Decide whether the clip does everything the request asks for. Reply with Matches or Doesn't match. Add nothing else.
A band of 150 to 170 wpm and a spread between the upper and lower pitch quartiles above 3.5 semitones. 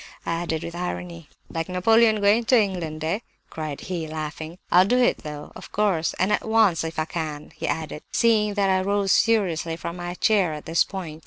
Doesn't match